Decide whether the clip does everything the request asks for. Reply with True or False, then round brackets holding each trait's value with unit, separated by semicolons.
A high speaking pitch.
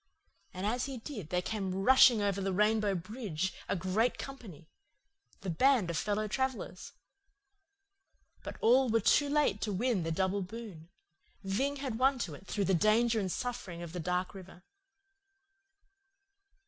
True (205 Hz)